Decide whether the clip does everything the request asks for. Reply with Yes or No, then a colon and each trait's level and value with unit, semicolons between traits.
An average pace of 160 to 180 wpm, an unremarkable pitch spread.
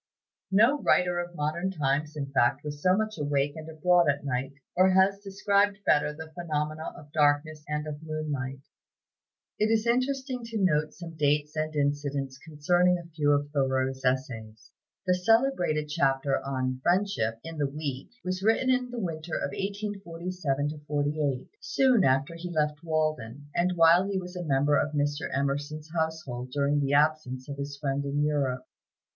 Yes: average, 165 wpm; average, 4.0 semitones